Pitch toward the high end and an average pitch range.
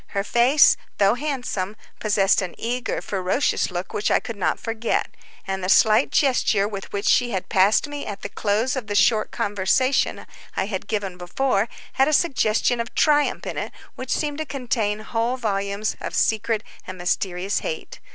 Yes: high, 215 Hz; average, 4.1 semitones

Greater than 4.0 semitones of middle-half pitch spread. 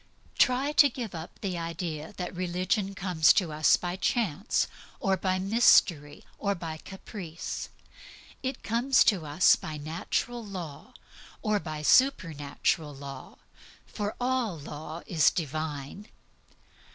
Yes: average, 5.1 semitones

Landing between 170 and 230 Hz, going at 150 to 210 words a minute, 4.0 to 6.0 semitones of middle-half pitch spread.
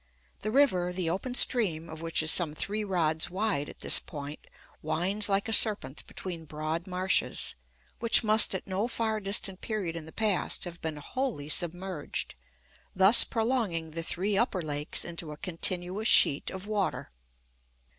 Yes: medium, 185 Hz; average, 160 wpm; average, 4.6 semitones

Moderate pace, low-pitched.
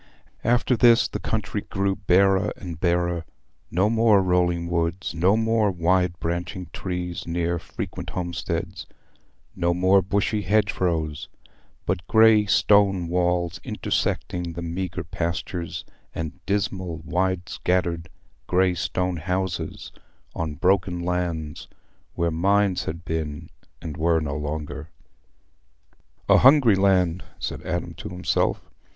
No: slow, 115 wpm; very low, 90 Hz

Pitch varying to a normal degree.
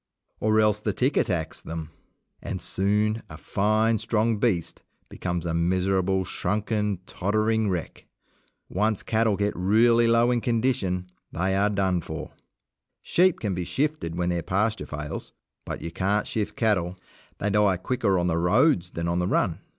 Yes: average, 3.6 semitones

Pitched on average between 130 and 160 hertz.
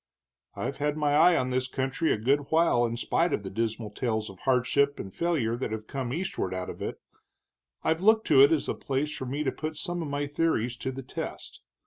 Yes: low, 135 Hz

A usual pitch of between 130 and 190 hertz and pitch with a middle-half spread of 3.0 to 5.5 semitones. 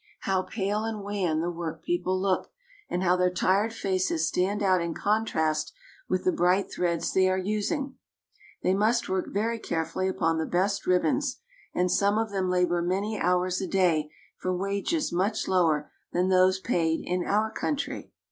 No: medium, 185 Hz; narrow, 2.5 semitones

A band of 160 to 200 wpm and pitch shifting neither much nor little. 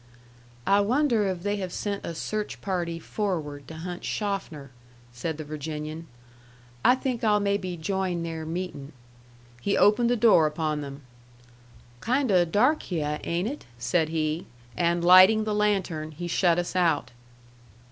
No: average, 150 wpm; average, 4.5 semitones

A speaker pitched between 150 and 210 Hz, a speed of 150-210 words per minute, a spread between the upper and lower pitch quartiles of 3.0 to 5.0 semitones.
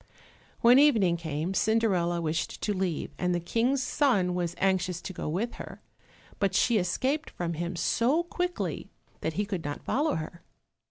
No: medium, 185 Hz; average, 165 wpm; wide, 5.4 semitones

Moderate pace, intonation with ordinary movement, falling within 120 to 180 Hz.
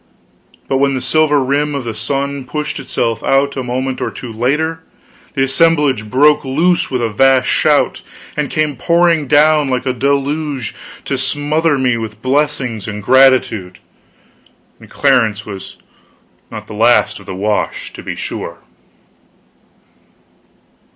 Yes: average, 145 wpm; average, 3.2 semitones; low, 135 Hz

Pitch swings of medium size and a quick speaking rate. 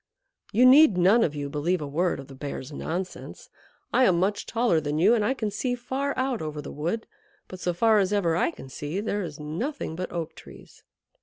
No: wide, 6.6 semitones; fast, 220 wpm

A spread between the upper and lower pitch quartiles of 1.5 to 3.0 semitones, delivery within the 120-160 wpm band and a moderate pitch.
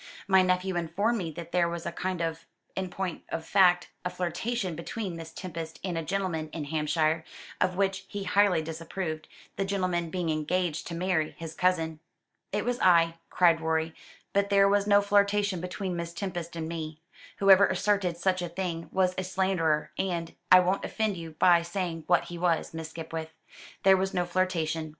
No: narrow, 2.6 semitones; average, 180 wpm; medium, 175 Hz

